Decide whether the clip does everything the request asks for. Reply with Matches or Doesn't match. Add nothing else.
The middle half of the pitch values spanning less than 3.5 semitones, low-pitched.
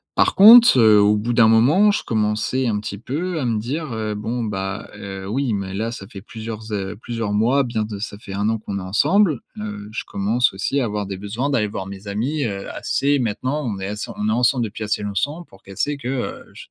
Doesn't match